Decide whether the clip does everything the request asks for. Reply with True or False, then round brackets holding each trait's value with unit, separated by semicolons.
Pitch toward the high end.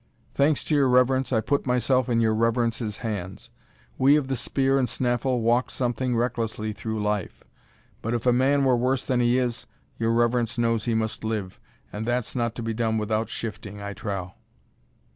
False (120 Hz)